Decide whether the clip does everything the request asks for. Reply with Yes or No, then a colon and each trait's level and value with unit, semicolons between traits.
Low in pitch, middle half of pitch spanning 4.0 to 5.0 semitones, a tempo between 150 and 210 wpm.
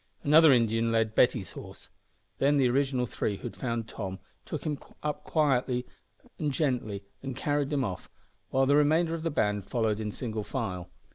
Yes: low, 125 Hz; average, 4.7 semitones; average, 170 wpm